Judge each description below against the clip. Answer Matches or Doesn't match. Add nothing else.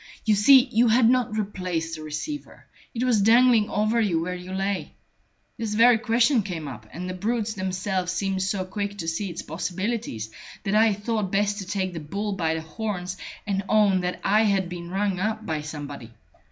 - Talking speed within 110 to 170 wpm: Doesn't match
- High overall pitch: Matches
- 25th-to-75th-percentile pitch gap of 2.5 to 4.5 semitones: Matches